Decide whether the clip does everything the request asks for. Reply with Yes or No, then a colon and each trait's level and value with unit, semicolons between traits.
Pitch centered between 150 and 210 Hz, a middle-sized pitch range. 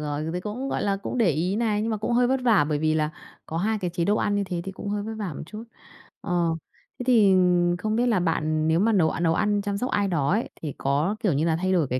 Yes: high, 190 Hz; average, 4.7 semitones